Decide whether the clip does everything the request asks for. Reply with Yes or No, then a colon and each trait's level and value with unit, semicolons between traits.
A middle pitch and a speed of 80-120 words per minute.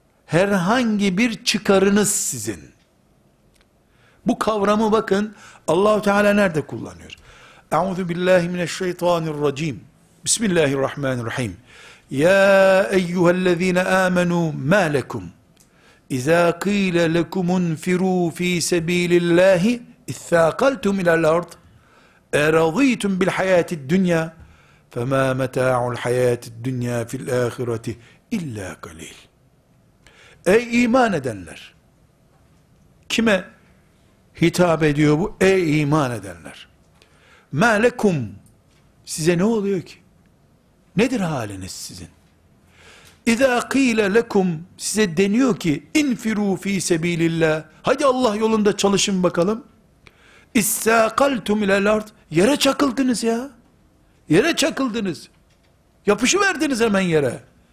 Yes: medium, 180 Hz; slow, 95 wpm